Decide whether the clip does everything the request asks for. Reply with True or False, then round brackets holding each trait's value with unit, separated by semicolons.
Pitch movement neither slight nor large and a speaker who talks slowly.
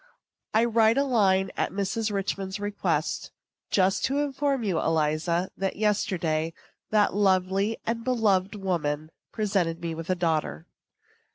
True (4.2 semitones; 130 wpm)